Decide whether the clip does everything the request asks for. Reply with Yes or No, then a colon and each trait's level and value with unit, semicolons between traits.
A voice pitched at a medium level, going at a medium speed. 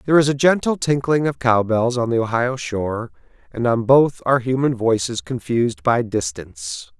No: low, 120 Hz; average, 170 wpm